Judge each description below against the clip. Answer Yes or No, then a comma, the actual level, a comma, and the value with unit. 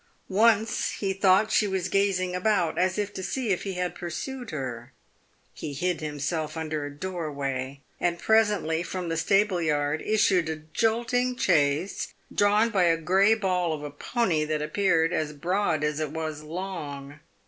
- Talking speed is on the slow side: No, average, 160 wpm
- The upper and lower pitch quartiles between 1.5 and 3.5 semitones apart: No, average, 4.6 semitones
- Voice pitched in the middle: Yes, medium, 175 Hz